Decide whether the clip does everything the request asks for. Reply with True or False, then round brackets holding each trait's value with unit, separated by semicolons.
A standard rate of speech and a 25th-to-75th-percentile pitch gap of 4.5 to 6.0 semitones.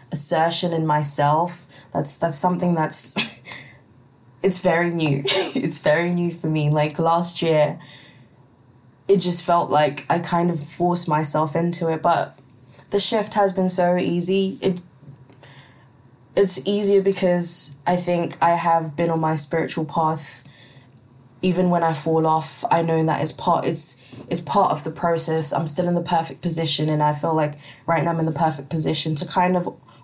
False (170 wpm; 3.3 semitones)